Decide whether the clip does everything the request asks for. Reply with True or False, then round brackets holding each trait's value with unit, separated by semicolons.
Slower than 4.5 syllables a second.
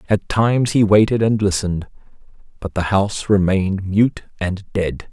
False (5.1 syllables/s)